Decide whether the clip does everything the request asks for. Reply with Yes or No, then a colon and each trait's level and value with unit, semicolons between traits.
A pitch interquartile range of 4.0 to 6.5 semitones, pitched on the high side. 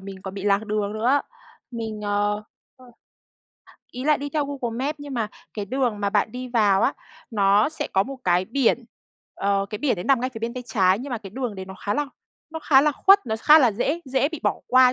Yes: average, 4.8 semitones; high, 230 Hz